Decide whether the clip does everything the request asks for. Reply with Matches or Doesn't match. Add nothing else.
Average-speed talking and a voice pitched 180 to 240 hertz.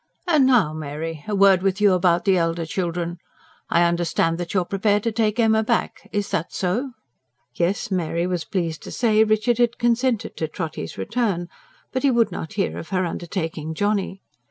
Matches